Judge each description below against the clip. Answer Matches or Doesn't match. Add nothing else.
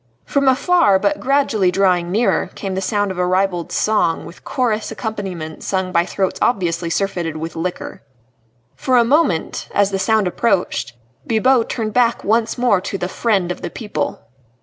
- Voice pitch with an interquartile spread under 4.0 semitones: Doesn't match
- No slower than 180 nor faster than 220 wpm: Doesn't match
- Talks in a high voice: Matches